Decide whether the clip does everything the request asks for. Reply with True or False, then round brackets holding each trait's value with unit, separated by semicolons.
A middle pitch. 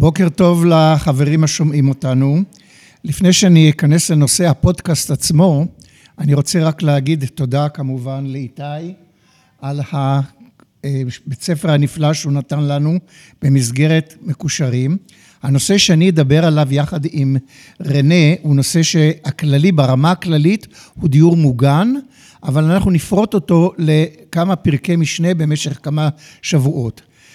True (155 Hz)